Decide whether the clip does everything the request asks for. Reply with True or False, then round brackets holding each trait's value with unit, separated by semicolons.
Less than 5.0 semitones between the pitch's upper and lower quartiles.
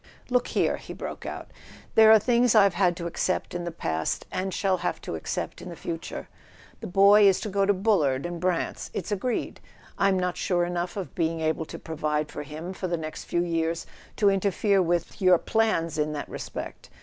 True (3.2 semitones)